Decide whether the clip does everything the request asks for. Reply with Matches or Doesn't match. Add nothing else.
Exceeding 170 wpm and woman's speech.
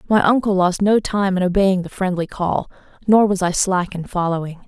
Matches